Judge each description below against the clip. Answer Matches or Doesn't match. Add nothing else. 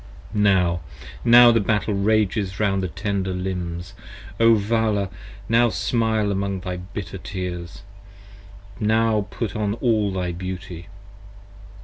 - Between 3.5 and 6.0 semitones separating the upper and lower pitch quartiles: Doesn't match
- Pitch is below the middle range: Matches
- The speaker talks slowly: Matches